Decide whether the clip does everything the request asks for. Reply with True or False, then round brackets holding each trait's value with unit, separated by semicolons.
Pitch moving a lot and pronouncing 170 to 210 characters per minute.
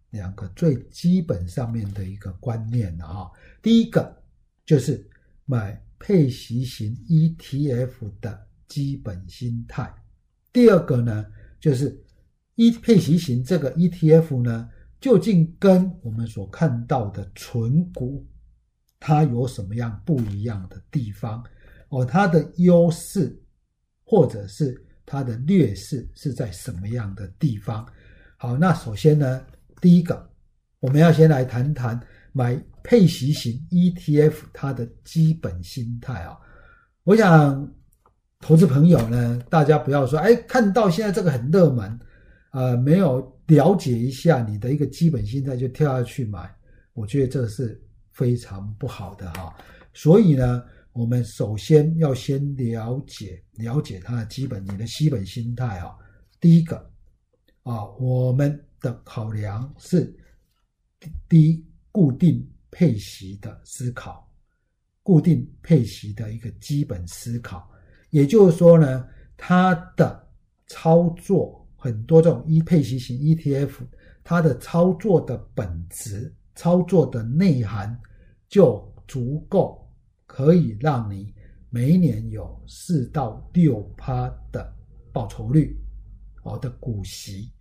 True (6.6 semitones; 195 characters per minute)